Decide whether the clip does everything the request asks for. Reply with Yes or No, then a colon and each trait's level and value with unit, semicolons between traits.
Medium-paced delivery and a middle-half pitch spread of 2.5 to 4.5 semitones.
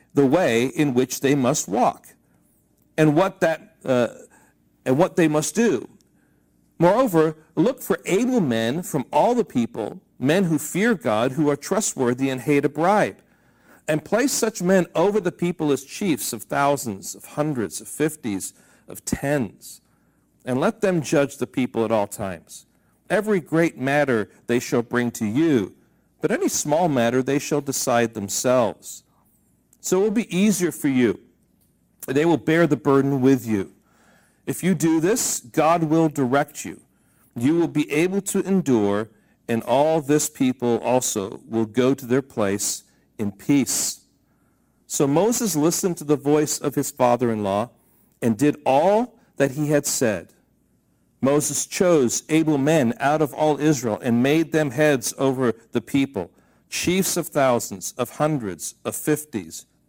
No: average, 160 wpm; average, 5.1 semitones